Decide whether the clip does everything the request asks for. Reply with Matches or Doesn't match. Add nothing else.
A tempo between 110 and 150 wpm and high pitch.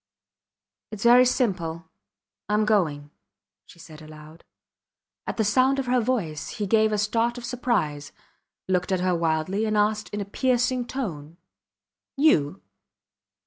Matches